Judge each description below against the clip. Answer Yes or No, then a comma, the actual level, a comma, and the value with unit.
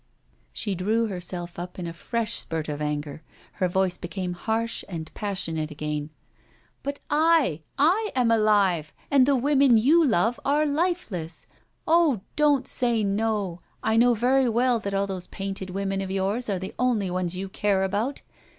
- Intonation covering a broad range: Yes, wide, 5.7 semitones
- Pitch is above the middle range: Yes, high, 200 Hz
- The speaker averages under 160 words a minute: No, average, 165 wpm